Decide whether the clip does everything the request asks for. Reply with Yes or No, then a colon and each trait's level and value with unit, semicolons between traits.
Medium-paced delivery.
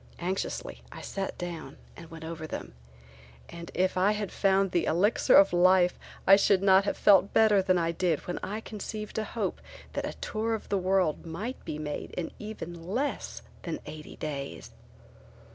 Yes: average, 180 wpm